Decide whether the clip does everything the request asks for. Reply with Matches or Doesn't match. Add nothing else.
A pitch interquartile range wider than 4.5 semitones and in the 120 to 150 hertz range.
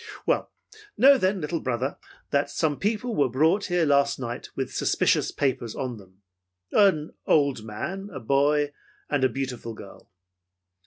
Matches